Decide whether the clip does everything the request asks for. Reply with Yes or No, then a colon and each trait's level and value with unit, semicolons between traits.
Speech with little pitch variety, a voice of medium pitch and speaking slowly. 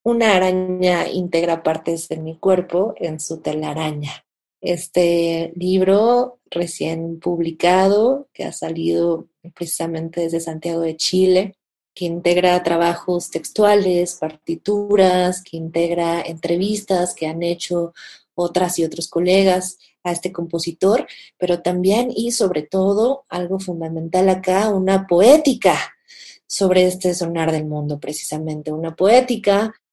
Yes: narrow, 2.2 semitones; medium, 175 Hz; slow, 115 wpm